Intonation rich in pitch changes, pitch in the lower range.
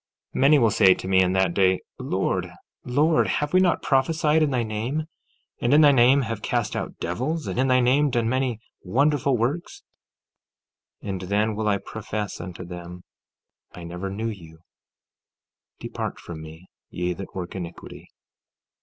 Yes: wide, 6.6 semitones; low, 110 Hz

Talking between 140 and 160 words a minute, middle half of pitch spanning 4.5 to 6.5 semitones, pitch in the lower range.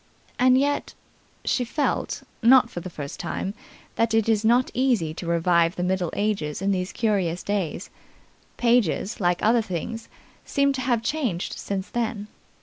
No: average, 155 wpm; average, 5.2 semitones; high, 210 Hz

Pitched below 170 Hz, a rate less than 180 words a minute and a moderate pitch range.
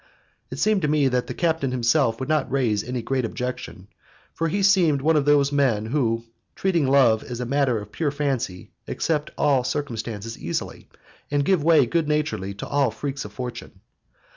No: low, 135 Hz; average, 190 wpm; average, 4.2 semitones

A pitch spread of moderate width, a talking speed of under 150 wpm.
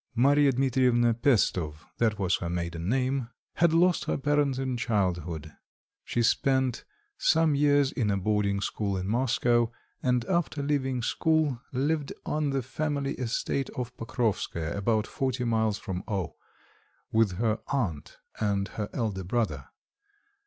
Yes: average, 5.0 semitones; average, 140 wpm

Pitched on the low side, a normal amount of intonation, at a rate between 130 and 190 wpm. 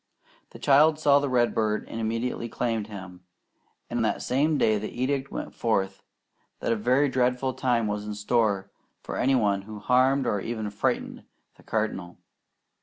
Yes: low, 115 Hz; average, 3.7 semitones; average, 165 wpm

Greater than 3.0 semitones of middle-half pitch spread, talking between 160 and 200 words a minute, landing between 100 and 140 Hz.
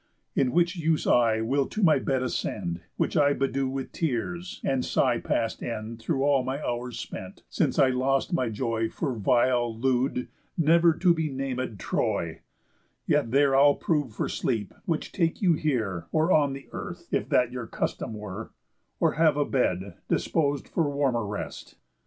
Yes: average, 4.2 semitones; average, 170 wpm; low, 135 Hz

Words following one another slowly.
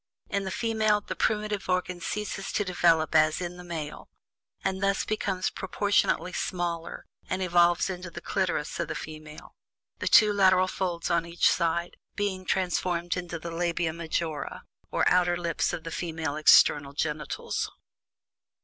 No: average, 150 wpm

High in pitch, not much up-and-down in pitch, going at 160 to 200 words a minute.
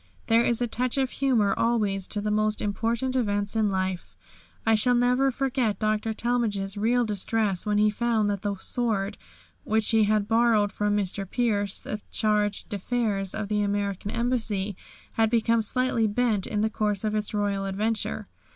Yes: high, 215 Hz; narrow, 2.3 semitones; average, 170 wpm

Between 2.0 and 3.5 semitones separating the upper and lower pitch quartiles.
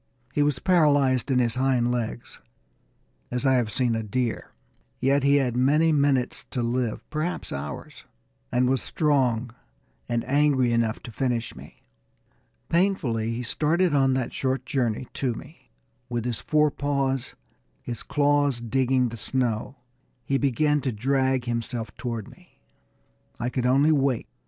Yes: average, 2.9 semitones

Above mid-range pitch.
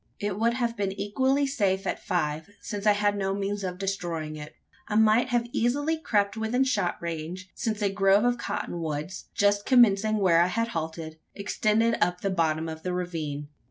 Yes: high, 200 Hz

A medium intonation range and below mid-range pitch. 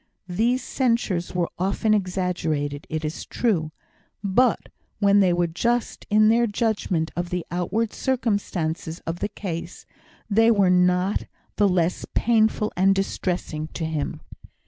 No: average, 4.2 semitones; high, 190 Hz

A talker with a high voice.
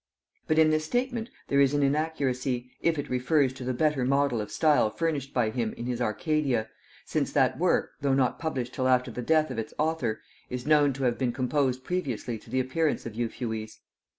No: low, 130 Hz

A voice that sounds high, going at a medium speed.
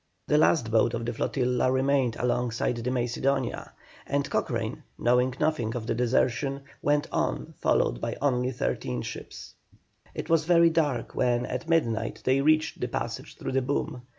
No: low, 125 Hz; average, 160 wpm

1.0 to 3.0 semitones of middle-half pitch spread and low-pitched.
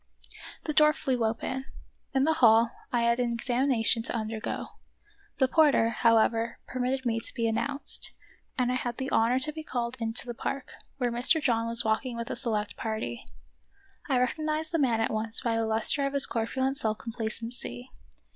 No: average, 2.7 semitones; high, 240 Hz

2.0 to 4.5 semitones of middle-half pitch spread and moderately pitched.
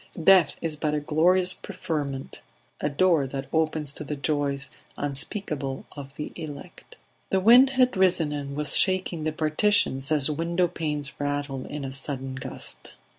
Yes: average, 3.6 semitones; medium, 150 Hz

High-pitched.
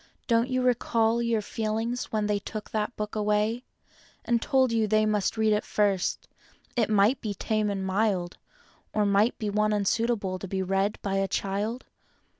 Yes: high, 215 Hz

